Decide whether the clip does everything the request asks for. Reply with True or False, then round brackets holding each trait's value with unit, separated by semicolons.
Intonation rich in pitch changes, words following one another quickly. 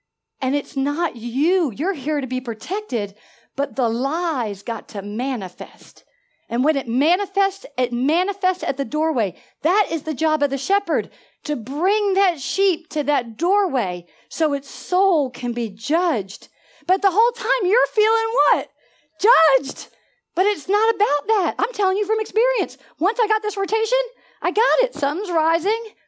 False (7.1 semitones; 165 wpm)